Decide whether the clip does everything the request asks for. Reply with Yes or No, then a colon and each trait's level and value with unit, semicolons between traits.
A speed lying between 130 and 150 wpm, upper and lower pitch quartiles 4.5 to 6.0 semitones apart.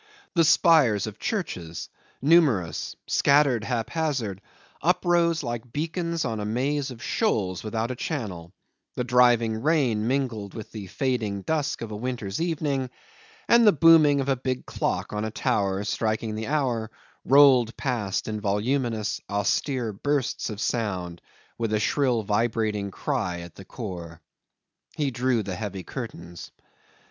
Yes: average, 140 wpm; average, 5.1 semitones